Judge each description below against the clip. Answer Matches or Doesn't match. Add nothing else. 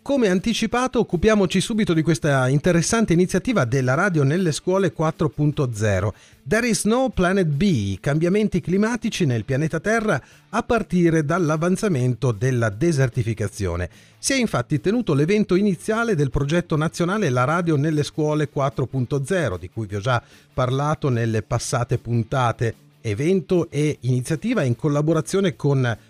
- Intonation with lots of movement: Matches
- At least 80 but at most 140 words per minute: Matches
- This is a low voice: Doesn't match